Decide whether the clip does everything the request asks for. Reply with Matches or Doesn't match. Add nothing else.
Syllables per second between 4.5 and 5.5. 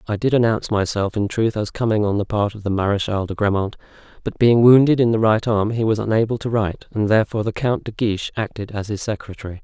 Doesn't match